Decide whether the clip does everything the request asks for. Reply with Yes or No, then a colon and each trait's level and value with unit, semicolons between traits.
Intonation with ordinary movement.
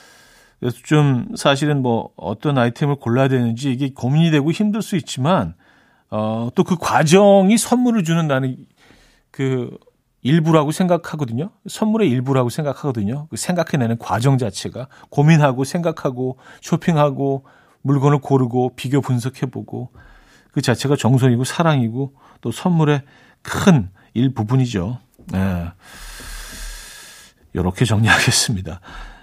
Yes: average, 4.5 semitones